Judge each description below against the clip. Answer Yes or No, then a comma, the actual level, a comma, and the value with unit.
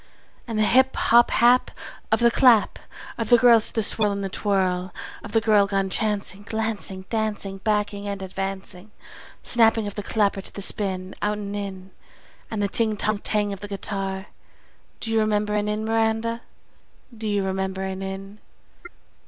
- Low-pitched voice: No, high, 205 Hz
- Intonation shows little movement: Yes, narrow, 2.3 semitones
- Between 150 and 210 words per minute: Yes, average, 175 wpm